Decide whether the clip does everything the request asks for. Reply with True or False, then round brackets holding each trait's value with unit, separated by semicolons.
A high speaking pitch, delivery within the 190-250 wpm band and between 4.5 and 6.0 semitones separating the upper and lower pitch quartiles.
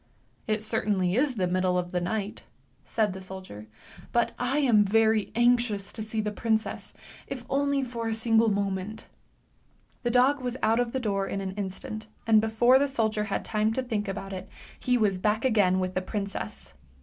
False (215 Hz; 195 wpm; 3.5 semitones)